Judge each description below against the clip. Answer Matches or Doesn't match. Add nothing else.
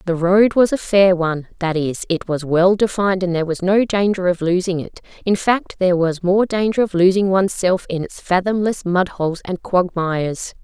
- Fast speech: Matches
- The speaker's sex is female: Matches